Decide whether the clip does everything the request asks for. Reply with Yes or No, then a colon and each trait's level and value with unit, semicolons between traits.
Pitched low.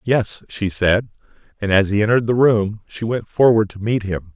Yes: low, 105 Hz